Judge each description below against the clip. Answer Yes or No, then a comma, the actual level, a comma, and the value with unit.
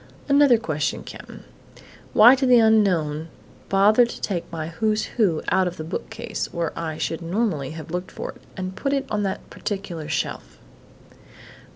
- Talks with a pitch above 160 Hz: Yes, high, 190 Hz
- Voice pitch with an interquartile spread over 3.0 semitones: Yes, average, 5.3 semitones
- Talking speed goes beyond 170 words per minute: No, average, 165 wpm